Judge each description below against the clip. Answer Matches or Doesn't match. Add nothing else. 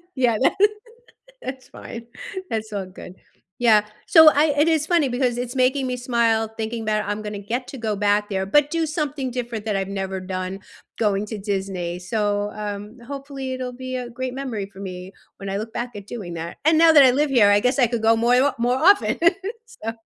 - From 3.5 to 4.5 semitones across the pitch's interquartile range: Matches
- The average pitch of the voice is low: Doesn't match